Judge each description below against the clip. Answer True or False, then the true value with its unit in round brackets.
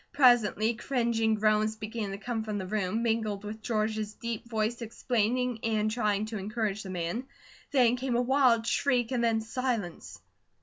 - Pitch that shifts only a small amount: True (2.1 semitones)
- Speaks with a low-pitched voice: False (220 Hz)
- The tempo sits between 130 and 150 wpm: False (165 wpm)